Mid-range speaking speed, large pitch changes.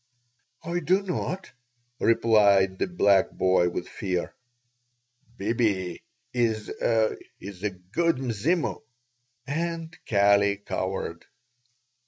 No: slow, 90 wpm; wide, 8.8 semitones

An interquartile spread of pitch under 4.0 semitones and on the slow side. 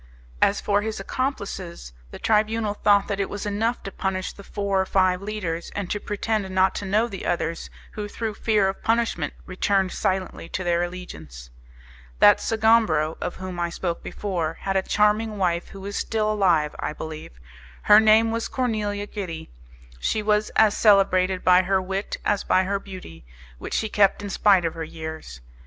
No: average, 2.8 semitones; average, 180 wpm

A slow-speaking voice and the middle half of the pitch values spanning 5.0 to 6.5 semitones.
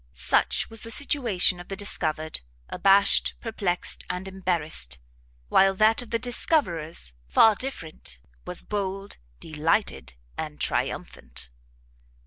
Yes: slow, 110 wpm; wide, 5.5 semitones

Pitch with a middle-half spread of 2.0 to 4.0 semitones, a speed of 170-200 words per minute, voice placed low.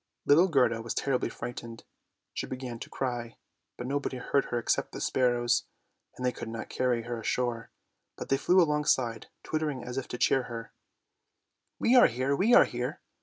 Yes: average, 2.8 semitones; average, 180 wpm; low, 125 Hz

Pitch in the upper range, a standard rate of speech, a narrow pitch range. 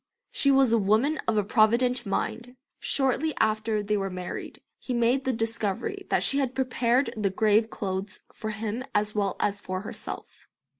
No: high, 225 Hz; average, 165 wpm; average, 3.5 semitones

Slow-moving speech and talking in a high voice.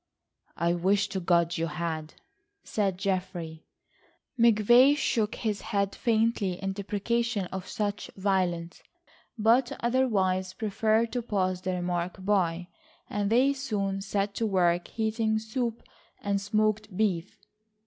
Yes: slow, 125 wpm; high, 200 Hz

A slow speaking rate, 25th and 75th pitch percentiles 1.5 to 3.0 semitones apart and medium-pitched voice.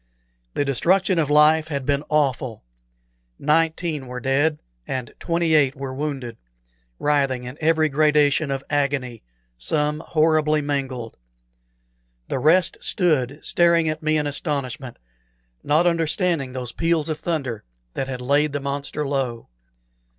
Yes: slow, 130 wpm; average, 2.7 semitones; medium, 145 Hz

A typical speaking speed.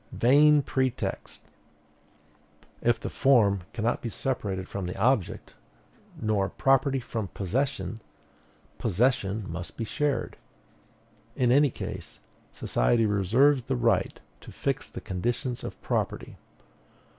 No: slow, 110 wpm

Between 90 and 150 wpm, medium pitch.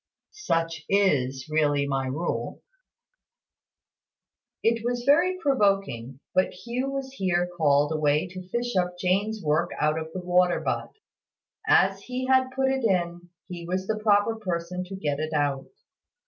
Yes: average, 145 wpm; medium, 180 Hz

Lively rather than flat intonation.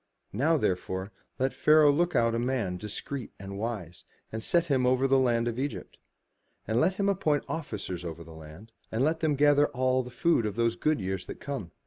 Yes: wide, 6.2 semitones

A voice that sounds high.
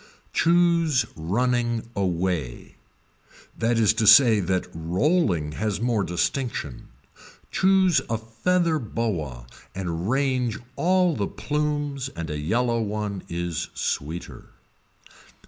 No: low, 110 Hz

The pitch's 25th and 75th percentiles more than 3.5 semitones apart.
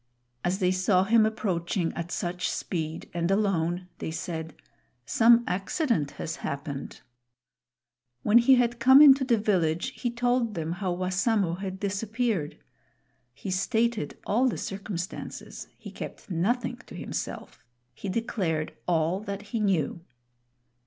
Yes: average, 5.0 semitones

